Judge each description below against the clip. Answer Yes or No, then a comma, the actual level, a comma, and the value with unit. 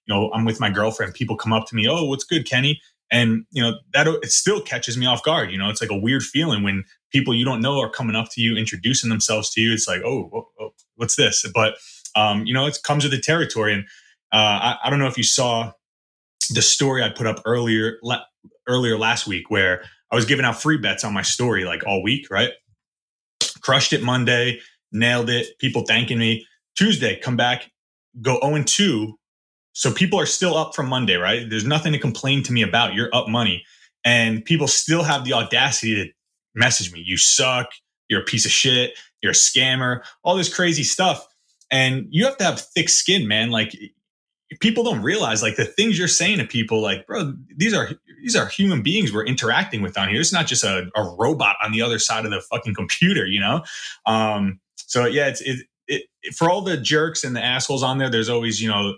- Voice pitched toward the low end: Yes, low, 120 Hz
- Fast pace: Yes, fast, 220 wpm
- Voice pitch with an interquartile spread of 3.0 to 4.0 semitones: No, average, 4.4 semitones